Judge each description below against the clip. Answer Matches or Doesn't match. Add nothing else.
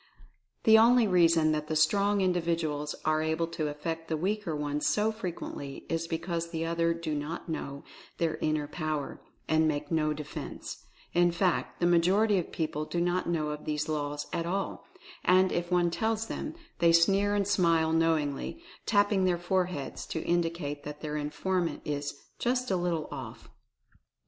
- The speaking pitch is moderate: Matches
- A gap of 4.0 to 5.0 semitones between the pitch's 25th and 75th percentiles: Doesn't match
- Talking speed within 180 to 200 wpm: Doesn't match